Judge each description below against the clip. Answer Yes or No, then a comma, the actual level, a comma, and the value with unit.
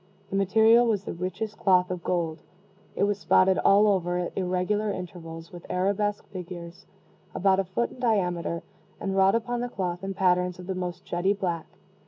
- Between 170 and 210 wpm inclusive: Yes, average, 180 wpm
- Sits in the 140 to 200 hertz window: Yes, medium, 185 Hz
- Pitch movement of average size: No, narrow, 2.3 semitones